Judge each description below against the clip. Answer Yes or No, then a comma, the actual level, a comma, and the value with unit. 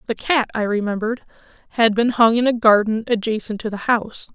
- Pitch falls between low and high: No, high, 225 Hz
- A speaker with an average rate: Yes, average, 195 wpm